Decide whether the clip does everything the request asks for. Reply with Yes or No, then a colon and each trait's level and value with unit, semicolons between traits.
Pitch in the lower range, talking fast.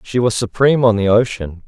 Yes: low, 115 Hz; fast, 215 wpm